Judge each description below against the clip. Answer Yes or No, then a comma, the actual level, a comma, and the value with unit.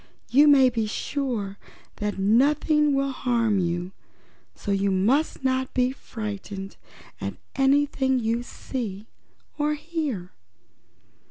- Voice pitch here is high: Yes, very high, 250 Hz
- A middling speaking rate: No, slow, 110 wpm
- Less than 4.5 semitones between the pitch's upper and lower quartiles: No, average, 5.3 semitones